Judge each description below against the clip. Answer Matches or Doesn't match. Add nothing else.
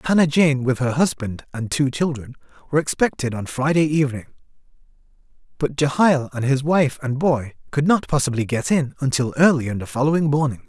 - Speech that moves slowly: Doesn't match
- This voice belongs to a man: Matches